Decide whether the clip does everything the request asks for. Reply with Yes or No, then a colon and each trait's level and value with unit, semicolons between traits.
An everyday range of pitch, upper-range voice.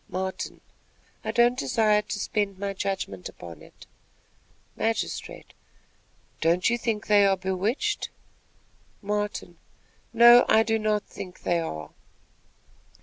Yes: average, 3.2 semitones; high, 205 Hz